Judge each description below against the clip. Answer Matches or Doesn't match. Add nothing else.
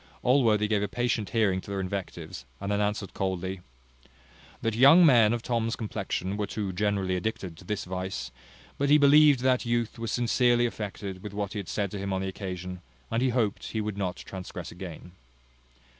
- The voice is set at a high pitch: Doesn't match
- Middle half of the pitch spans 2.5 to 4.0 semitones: Matches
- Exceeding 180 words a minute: Matches